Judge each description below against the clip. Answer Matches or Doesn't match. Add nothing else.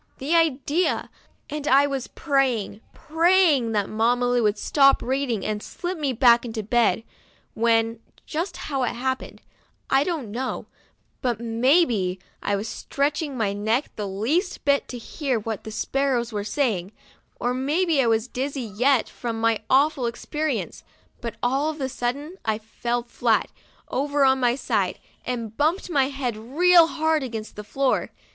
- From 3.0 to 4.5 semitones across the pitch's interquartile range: Matches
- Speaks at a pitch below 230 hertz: Doesn't match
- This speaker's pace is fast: Doesn't match